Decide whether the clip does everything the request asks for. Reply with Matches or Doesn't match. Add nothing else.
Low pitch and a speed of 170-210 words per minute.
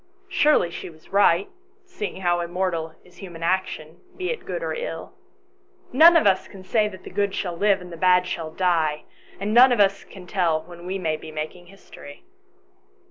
Doesn't match